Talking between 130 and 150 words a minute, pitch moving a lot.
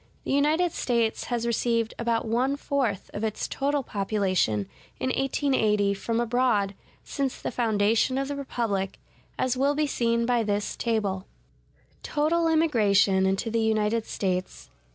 No: average, 140 wpm; average, 4.7 semitones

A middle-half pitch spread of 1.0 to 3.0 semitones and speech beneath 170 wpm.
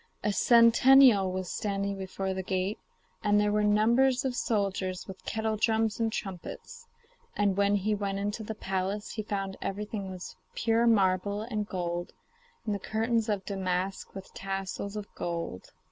Yes: narrow, 2.4 semitones; average, 160 wpm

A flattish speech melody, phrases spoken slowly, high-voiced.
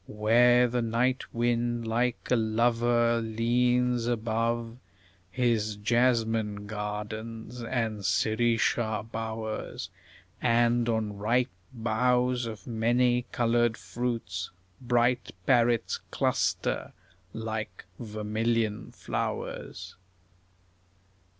No: narrow, 1.7 semitones; slow, 80 wpm; low, 115 Hz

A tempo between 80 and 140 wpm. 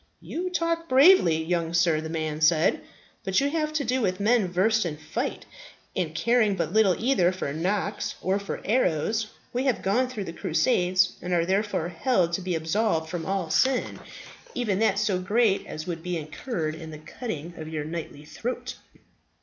No: average, 180 wpm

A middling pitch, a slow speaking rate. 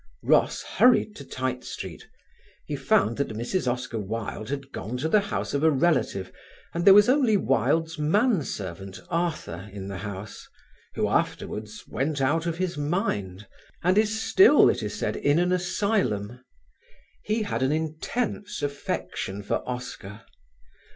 No: medium, 145 Hz; average, 150 wpm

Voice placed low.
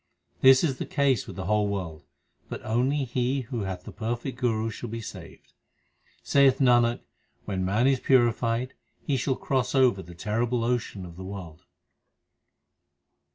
Yes: low, 120 Hz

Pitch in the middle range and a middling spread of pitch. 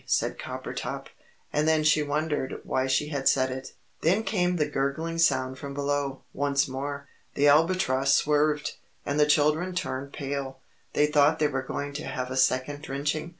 No: medium, 145 Hz; narrow, 2.0 semitones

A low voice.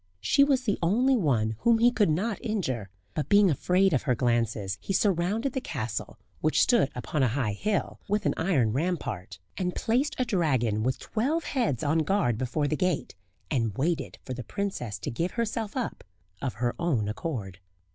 No: medium, 165 Hz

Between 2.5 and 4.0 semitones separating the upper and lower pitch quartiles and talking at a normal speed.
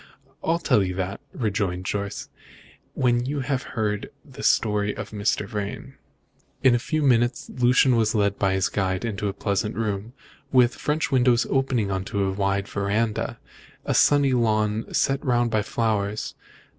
Yes: average, 3.7 semitones; average, 165 wpm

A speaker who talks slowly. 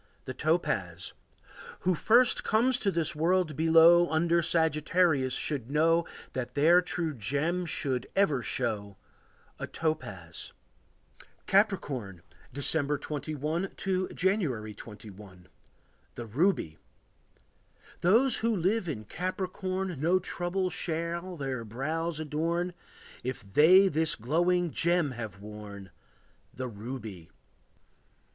Yes: slow, 105 wpm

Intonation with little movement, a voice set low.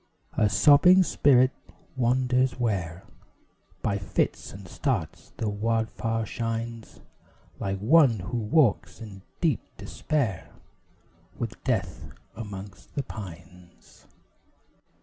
No: average, 4.6 semitones; low, 115 Hz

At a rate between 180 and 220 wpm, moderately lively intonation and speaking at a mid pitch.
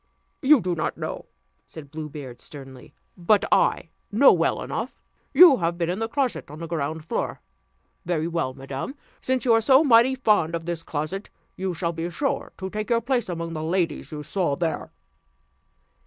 No: average, 185 wpm; wide, 6.3 semitones; medium, 170 Hz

